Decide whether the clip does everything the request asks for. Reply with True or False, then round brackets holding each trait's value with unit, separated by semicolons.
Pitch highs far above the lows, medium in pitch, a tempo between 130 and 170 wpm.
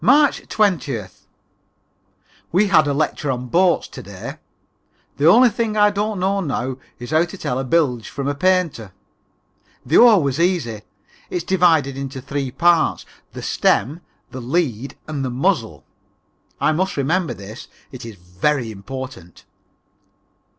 True (6.3 semitones; 145 Hz; 150 wpm)